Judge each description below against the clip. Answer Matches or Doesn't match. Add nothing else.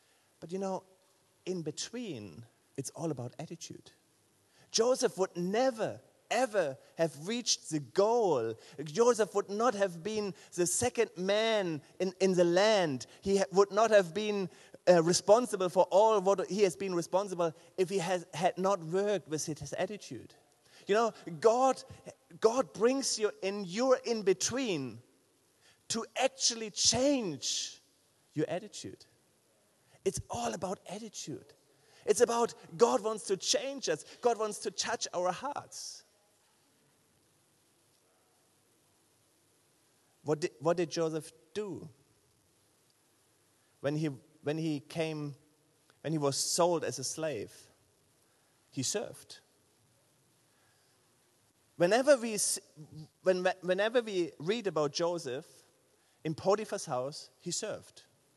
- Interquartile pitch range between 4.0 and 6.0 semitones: Matches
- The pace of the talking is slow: Matches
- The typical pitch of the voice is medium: Matches